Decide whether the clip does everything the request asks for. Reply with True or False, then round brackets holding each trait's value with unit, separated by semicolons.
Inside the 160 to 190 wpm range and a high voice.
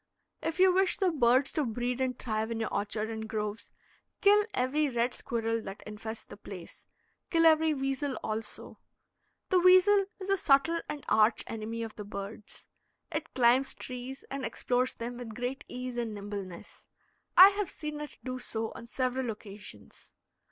True (165 wpm; 250 Hz)